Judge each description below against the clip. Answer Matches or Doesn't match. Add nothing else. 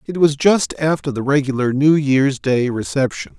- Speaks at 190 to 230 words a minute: Doesn't match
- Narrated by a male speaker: Matches